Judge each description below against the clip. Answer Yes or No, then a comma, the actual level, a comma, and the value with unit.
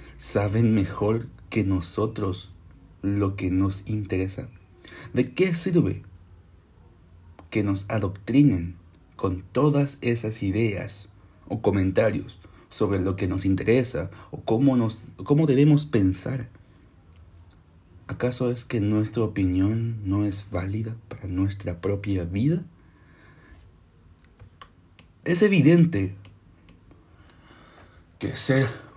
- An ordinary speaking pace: No, slow, 100 wpm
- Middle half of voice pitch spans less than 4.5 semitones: Yes, average, 4.1 semitones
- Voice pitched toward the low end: Yes, low, 100 Hz